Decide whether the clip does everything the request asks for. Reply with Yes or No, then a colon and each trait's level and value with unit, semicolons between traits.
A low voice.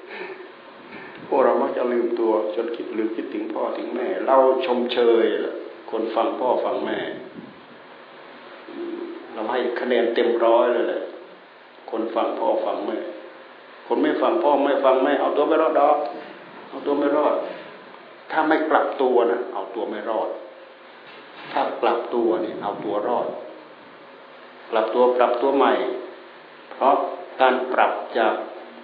No: very high, 340 Hz